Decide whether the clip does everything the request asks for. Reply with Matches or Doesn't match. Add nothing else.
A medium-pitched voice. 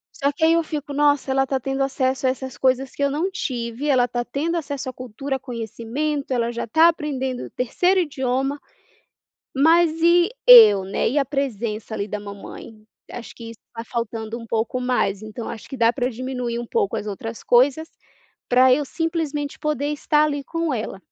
Doesn't match